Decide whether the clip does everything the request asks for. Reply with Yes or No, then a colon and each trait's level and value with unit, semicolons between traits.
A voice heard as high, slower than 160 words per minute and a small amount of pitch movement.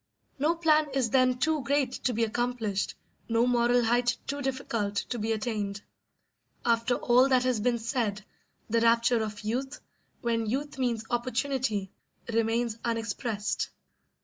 Yes: high, 240 Hz; average, 140 wpm; narrow, 2.3 semitones